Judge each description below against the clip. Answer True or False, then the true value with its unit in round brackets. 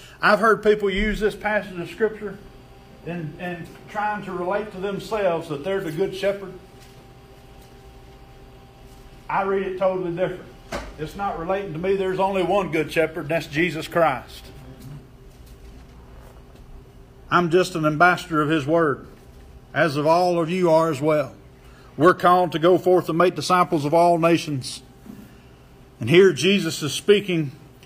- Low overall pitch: False (165 Hz)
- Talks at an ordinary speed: True (150 wpm)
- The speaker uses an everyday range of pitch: False (6.2 semitones)